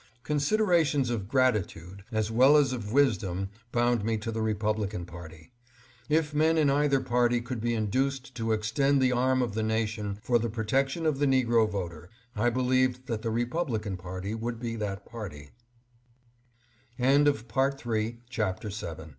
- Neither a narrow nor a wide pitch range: Yes, average, 3.8 semitones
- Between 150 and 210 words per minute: No, average, 140 wpm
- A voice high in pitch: No, low, 120 Hz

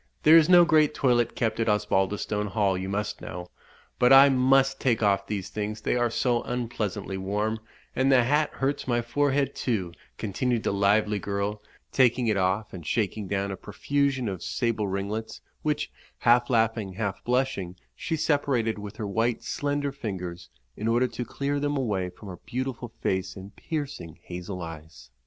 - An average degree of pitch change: Yes, average, 4.8 semitones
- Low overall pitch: Yes, low, 110 Hz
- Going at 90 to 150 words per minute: No, average, 170 wpm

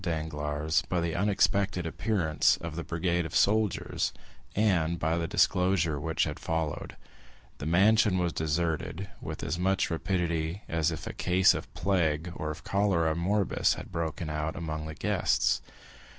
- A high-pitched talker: No, very low, 85 Hz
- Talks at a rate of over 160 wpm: No, average, 150 wpm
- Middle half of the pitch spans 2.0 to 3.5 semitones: Yes, average, 2.9 semitones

